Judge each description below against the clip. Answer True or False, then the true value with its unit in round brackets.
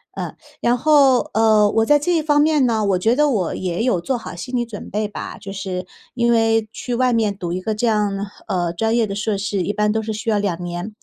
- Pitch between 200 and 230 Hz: True (215 Hz)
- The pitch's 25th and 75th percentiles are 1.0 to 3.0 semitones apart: False (3.4 semitones)